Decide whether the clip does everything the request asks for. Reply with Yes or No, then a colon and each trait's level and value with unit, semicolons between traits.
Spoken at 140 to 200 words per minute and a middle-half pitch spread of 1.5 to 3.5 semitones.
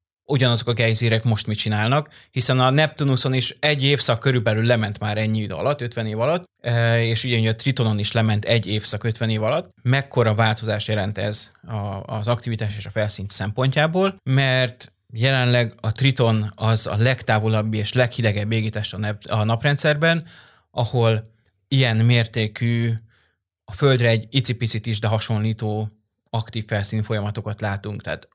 Yes: average, 145 wpm; average, 2.9 semitones